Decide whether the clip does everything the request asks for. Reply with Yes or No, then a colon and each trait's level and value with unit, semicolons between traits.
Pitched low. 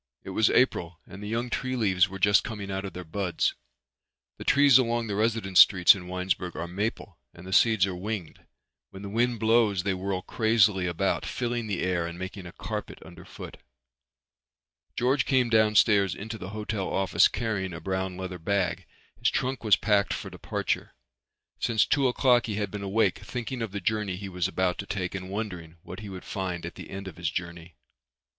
Yes: low, 100 Hz